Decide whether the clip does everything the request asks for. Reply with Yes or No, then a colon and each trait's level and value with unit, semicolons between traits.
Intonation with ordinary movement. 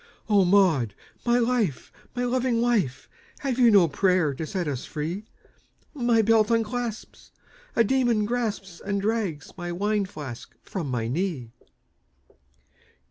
No: wide, 5.9 semitones